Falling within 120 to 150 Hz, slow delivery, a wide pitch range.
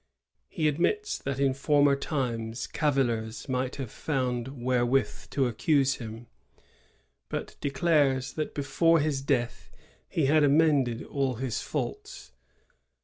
No: low, 135 Hz; slow, 120 wpm; average, 2.9 semitones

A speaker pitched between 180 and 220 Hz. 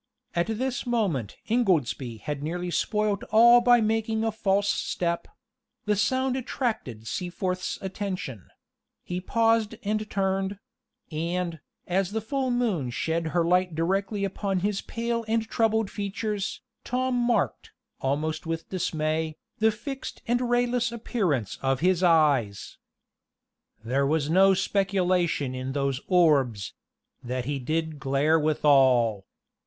Yes: medium, 185 Hz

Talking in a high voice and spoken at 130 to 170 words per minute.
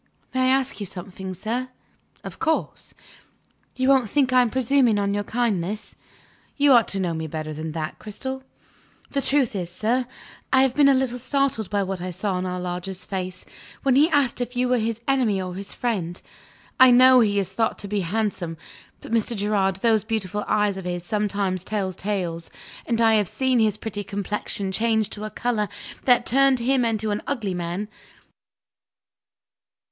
No: high, 215 Hz; average, 185 wpm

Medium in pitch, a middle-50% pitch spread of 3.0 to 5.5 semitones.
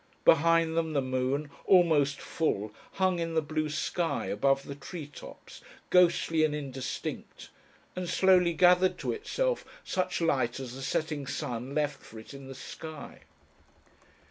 Yes: medium, 150 Hz; average, 3.6 semitones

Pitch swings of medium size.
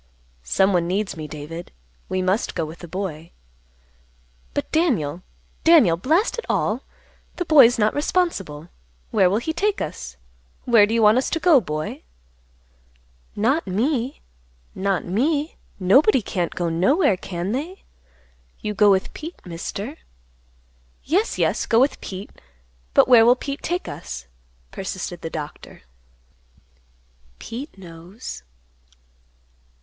No: wide, 8.4 semitones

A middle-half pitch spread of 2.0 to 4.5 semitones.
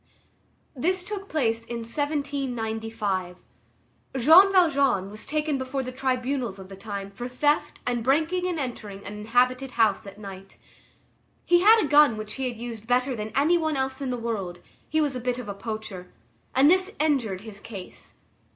No: average, 5.2 semitones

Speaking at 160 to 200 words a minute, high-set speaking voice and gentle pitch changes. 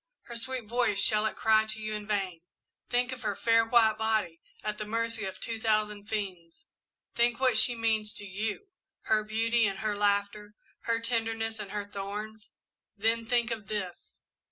Yes: average, 180 wpm; high, 220 Hz; narrow, 1.7 semitones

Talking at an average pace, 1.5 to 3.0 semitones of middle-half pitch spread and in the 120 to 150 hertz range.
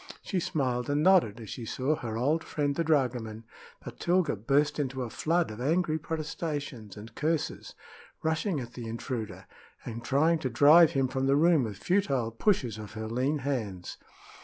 No: average, 175 wpm; wide, 5.4 semitones; low, 135 Hz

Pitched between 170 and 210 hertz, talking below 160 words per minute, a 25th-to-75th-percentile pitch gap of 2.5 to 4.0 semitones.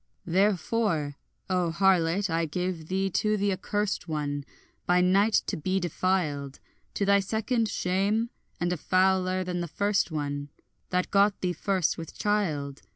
Yes: medium, 185 Hz; average, 150 wpm; average, 3.4 semitones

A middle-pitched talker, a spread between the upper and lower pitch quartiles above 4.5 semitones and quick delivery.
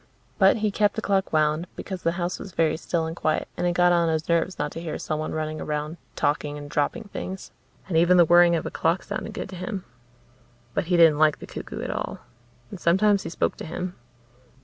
No: medium, 170 Hz; average, 2.9 semitones; fast, 225 wpm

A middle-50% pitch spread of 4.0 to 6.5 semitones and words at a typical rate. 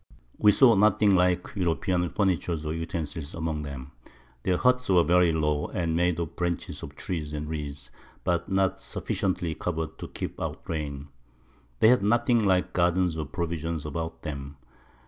No: average, 3.3 semitones; average, 160 wpm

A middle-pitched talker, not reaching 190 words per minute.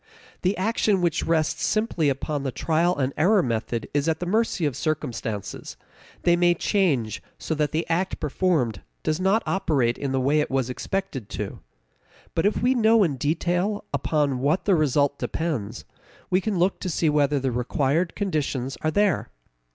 Yes: medium, 155 Hz; average, 175 wpm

